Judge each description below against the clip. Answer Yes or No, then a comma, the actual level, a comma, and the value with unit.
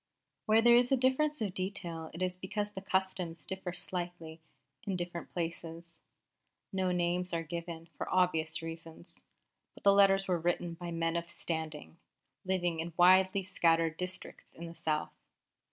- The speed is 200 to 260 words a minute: No, average, 155 wpm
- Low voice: No, medium, 175 Hz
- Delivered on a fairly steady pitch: Yes, narrow, 2.3 semitones